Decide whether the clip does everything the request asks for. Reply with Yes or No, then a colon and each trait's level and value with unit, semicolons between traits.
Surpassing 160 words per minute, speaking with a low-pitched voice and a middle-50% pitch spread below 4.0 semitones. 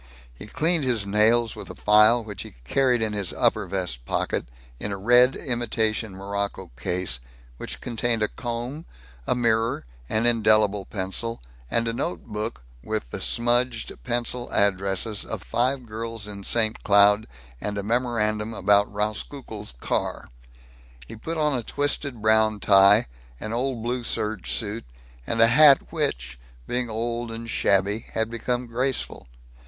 No: average, 150 wpm; low, 110 Hz; average, 2.8 semitones